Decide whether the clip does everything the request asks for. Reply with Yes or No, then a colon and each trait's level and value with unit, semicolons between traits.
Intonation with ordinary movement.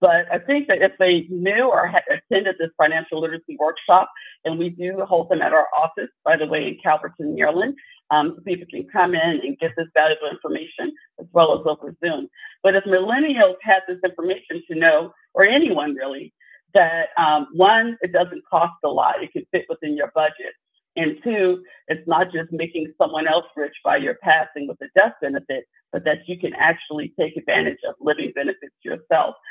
Yes: average, 3.3 semitones